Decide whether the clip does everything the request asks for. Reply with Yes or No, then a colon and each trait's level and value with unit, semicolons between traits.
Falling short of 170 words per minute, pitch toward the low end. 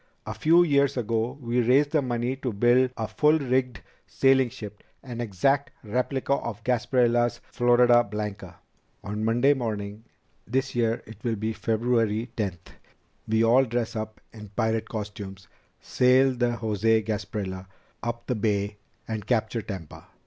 Yes: average, 145 wpm; low, 115 Hz